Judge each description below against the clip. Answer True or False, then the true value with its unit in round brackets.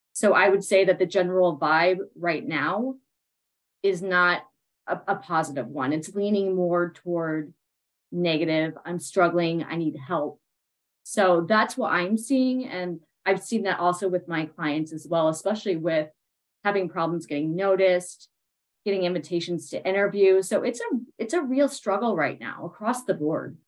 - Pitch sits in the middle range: True (180 Hz)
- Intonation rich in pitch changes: False (3.4 semitones)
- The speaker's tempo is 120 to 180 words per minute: True (160 wpm)